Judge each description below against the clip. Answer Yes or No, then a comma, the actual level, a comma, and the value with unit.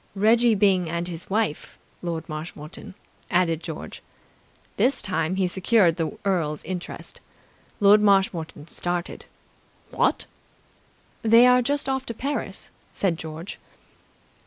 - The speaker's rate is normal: No, slow, 115 wpm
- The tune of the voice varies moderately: Yes, average, 4.7 semitones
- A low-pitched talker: No, medium, 185 Hz